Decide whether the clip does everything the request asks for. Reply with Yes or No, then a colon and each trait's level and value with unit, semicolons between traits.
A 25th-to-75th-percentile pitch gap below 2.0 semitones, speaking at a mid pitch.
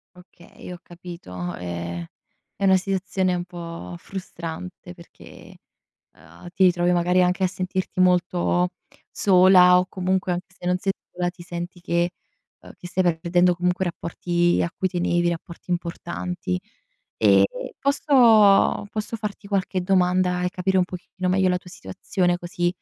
Yes: narrow, 1.2 semitones; medium, 180 Hz